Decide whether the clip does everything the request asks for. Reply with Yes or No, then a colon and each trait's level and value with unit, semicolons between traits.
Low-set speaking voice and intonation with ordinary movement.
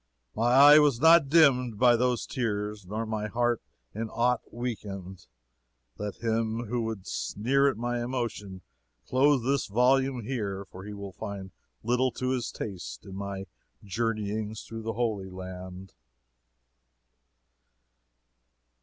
Yes: low, 115 Hz; average, 3.6 semitones